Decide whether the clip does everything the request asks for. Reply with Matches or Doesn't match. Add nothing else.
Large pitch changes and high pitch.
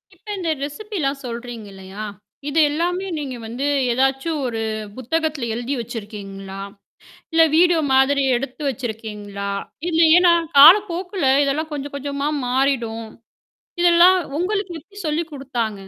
Matches